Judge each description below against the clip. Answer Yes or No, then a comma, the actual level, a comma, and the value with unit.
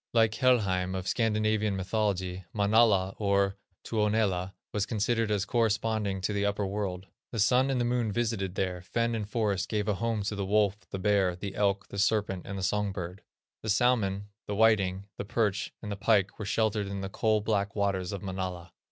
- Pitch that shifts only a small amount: Yes, narrow, 2.2 semitones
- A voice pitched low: Yes, low, 100 Hz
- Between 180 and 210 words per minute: Yes, average, 185 wpm